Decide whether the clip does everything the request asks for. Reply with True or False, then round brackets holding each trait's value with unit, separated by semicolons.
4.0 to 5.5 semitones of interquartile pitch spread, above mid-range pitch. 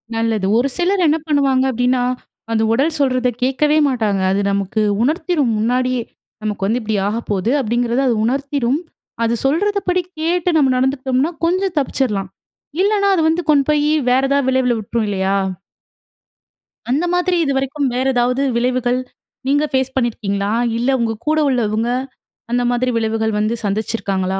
True (4.3 semitones; 255 Hz)